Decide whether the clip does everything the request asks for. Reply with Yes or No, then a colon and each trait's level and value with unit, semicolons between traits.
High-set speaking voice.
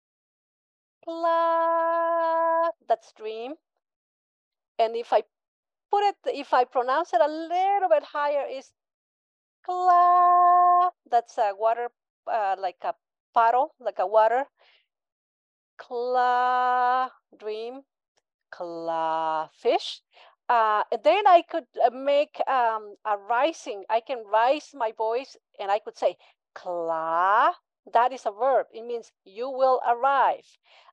Yes: very high, 255 Hz